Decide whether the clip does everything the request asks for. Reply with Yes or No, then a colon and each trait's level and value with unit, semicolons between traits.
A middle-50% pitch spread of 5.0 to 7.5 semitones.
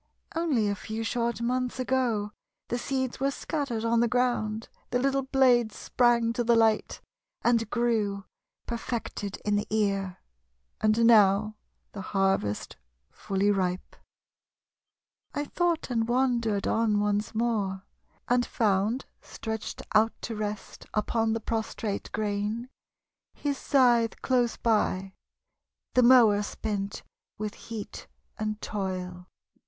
No: average, 2.8 semitones